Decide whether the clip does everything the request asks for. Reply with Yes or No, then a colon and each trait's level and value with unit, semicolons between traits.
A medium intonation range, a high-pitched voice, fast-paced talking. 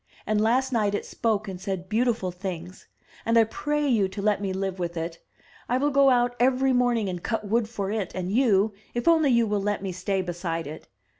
Yes: average, 4.4 semitones; high, 210 Hz; fast, 220 wpm